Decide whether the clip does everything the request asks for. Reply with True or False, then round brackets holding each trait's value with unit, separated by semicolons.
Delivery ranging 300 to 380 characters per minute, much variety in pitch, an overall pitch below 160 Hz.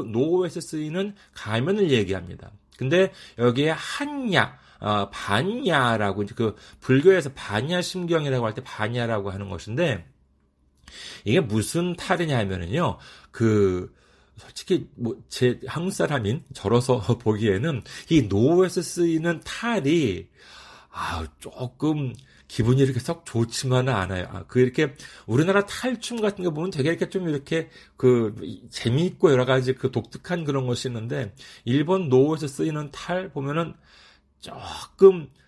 False (285 characters per minute; 7.2 semitones; 135 Hz)